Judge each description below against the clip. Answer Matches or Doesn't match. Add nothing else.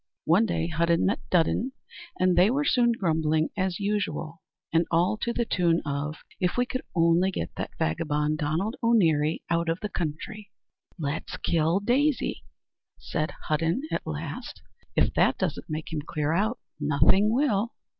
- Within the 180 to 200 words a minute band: Doesn't match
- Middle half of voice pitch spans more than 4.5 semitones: Matches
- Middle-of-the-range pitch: Matches